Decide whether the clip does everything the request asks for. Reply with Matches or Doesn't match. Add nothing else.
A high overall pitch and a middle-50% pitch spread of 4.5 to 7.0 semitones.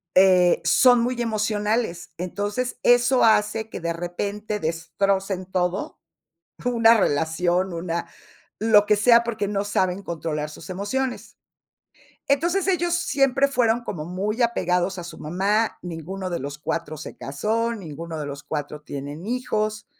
Matches